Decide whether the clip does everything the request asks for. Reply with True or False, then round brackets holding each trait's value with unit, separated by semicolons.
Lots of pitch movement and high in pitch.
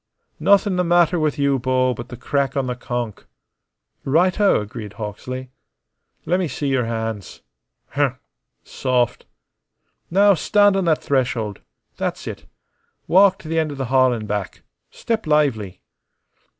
False (6.3 semitones; 135 Hz)